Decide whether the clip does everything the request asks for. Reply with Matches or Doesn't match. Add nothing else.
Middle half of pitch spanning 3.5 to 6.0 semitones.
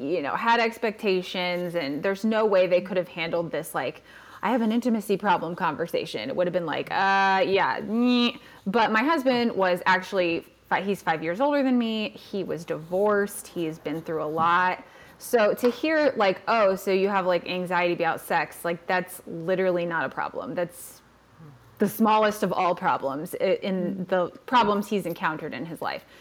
Matches